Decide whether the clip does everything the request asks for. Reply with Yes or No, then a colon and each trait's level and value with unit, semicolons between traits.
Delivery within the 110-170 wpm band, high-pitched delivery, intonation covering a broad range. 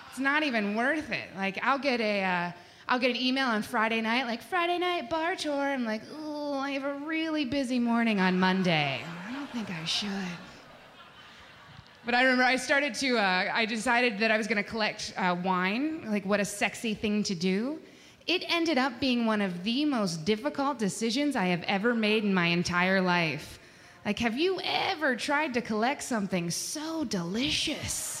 No: average, 190 wpm; high, 230 Hz; wide, 6.0 semitones